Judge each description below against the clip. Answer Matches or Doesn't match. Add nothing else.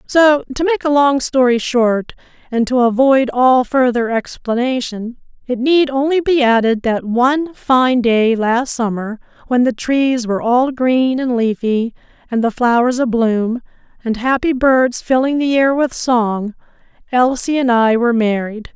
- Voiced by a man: Doesn't match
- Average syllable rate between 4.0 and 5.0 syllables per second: Matches